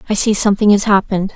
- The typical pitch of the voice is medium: No, high, 205 Hz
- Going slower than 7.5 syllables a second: No, 7.7 syllables/s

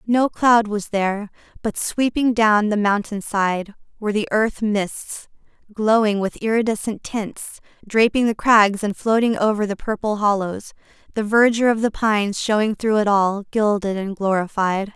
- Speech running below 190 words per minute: Yes, average, 155 wpm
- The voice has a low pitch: No, high, 210 Hz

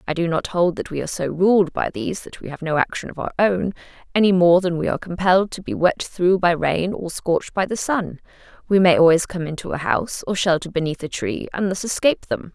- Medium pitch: Yes, medium, 180 Hz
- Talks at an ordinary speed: No, fast, 250 wpm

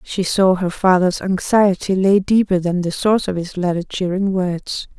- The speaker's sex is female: Yes, female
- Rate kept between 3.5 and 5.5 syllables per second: Yes, 4.6 syllables/s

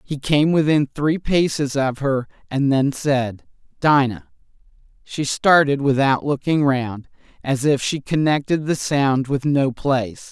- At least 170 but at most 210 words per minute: No, average, 145 wpm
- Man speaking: No, female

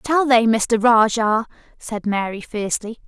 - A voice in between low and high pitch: No, high, 225 Hz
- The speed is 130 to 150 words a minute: Yes, slow, 135 wpm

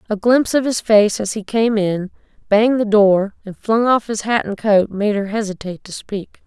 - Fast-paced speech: Yes, fast, 225 wpm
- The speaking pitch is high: Yes, high, 210 Hz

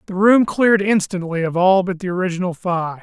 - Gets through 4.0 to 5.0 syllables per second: No, 5.6 syllables/s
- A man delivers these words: Yes, male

